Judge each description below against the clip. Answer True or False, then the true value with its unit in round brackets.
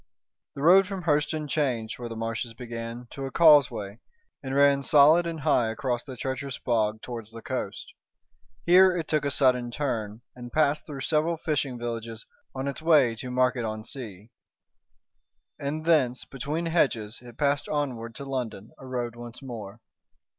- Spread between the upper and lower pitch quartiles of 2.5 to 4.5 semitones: True (4.2 semitones)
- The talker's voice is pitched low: True (130 Hz)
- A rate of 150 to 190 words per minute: True (165 wpm)